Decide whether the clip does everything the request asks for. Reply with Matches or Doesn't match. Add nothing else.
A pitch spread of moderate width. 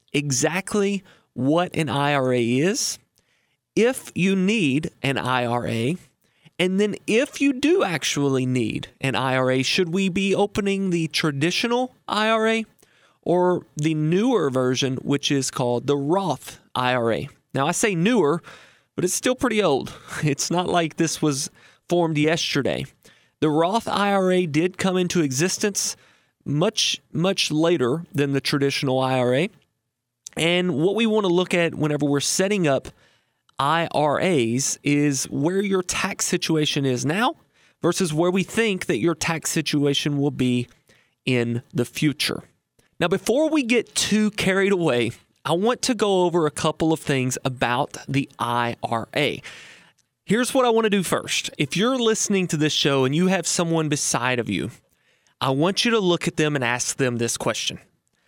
Doesn't match